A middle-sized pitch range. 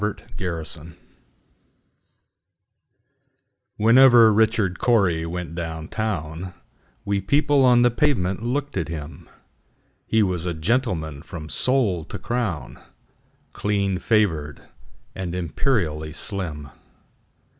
No: wide, 5.9 semitones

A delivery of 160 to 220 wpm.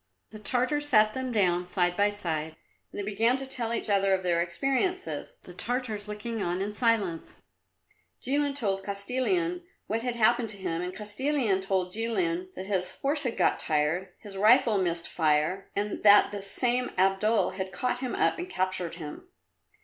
Yes: average, 175 wpm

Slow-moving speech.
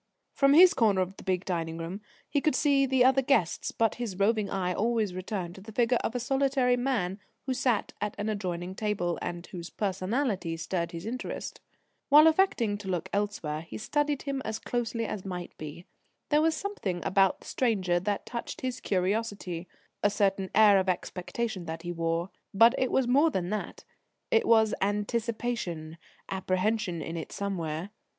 No: average, 175 wpm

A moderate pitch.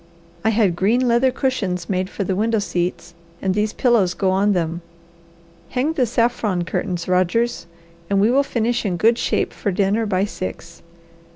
No: high, 205 Hz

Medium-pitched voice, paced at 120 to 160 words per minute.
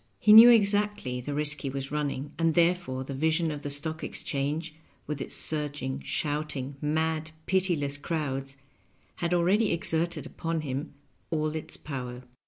Yes: medium, 150 Hz; average, 150 wpm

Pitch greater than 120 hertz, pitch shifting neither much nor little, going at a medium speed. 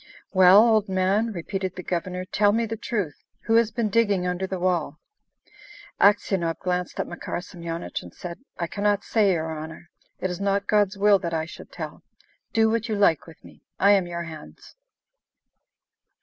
Yes: high, 190 Hz; average, 3.2 semitones; average, 180 wpm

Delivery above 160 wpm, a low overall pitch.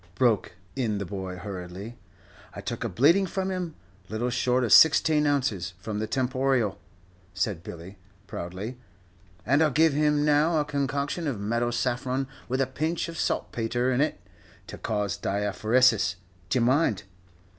No: average, 150 wpm; low, 125 Hz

